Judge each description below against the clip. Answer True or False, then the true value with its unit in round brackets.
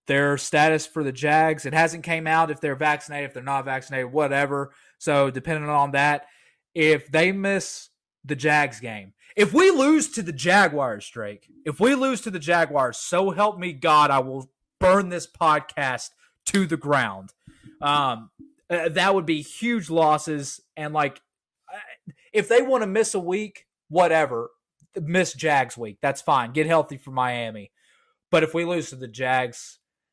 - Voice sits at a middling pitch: True (155 Hz)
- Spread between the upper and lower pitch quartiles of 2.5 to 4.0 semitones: False (4.5 semitones)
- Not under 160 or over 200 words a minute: True (170 wpm)